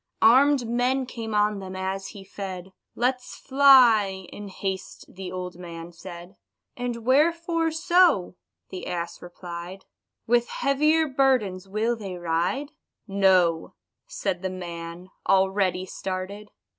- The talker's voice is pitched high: Yes, high, 195 Hz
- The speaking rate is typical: No, slow, 120 wpm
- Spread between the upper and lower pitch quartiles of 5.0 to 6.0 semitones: Yes, wide, 5.4 semitones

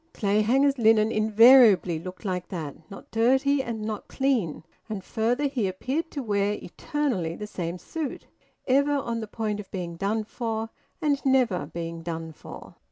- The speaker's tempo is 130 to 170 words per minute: Yes, average, 160 wpm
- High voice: Yes, high, 220 Hz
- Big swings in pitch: Yes, wide, 5.9 semitones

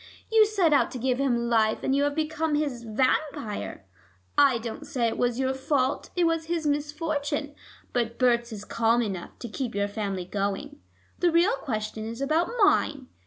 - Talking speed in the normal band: Yes, average, 180 wpm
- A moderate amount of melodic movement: Yes, average, 4.7 semitones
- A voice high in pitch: Yes, very high, 265 Hz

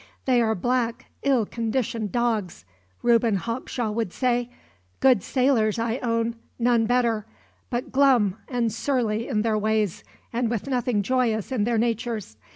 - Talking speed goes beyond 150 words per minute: No, average, 145 wpm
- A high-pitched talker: Yes, high, 230 Hz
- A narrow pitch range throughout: Yes, narrow, 2.2 semitones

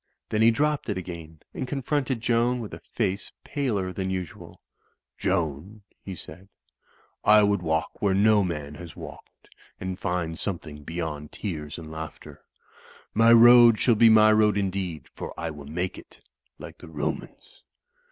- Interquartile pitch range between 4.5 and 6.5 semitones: Yes, average, 5.1 semitones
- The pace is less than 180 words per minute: Yes, average, 155 wpm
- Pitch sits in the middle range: No, very low, 95 Hz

